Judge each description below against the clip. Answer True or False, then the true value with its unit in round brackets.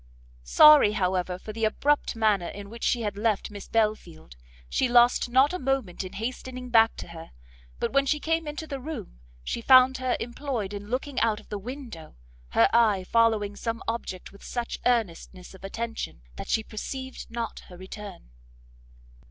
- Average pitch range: True (4.2 semitones)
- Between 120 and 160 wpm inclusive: False (175 wpm)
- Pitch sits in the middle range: False (225 Hz)